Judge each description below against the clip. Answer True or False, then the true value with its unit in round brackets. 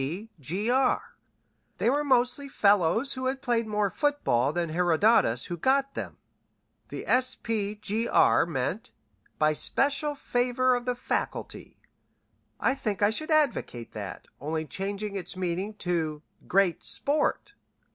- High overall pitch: True (215 Hz)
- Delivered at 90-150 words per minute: True (135 wpm)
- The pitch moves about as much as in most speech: False (6.7 semitones)